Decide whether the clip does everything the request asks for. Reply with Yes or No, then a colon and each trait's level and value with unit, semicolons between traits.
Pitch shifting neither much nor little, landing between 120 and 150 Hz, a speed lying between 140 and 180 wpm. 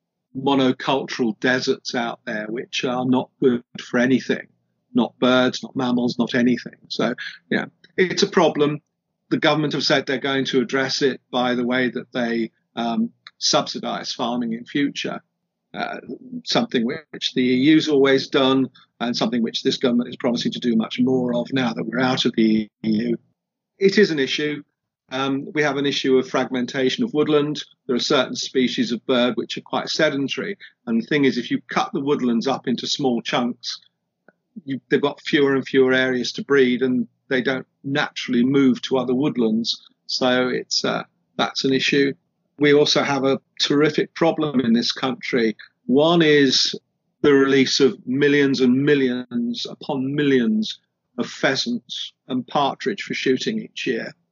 Yes: average, 3.0 semitones; low, 135 Hz; average, 170 wpm